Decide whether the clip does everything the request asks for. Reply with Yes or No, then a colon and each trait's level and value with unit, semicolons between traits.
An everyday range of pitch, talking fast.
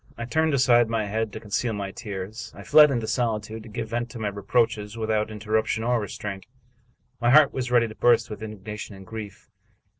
No: narrow, 2.2 semitones; fast, 210 wpm